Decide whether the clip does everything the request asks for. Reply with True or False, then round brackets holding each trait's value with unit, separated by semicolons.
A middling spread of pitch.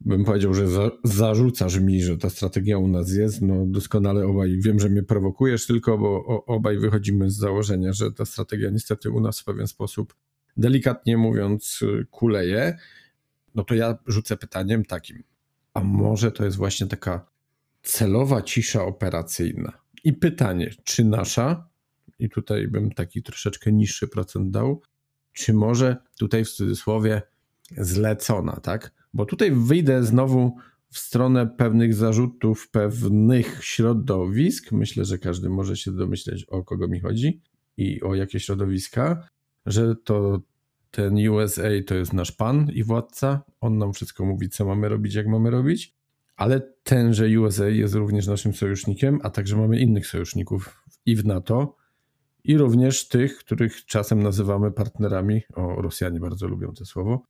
True (3.6 semitones)